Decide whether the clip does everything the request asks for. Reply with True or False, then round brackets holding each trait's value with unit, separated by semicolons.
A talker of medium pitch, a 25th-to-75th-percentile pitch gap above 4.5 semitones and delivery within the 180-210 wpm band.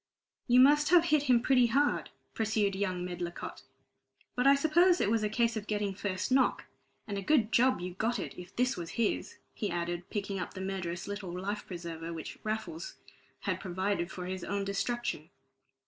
False (205 Hz; 5.1 semitones; 190 wpm)